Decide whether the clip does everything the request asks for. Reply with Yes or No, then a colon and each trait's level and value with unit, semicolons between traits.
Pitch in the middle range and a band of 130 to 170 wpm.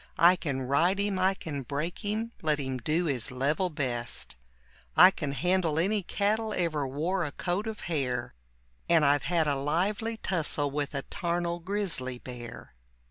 Yes: medium, 165 Hz; average, 165 wpm